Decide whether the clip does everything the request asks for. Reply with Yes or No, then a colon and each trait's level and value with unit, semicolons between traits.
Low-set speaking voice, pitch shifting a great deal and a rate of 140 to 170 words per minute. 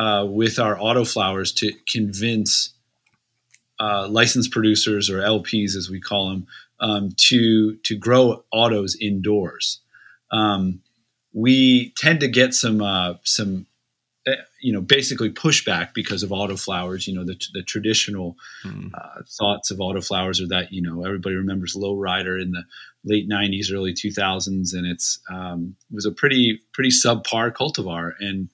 No: low, 105 Hz; average, 3.2 semitones; average, 150 wpm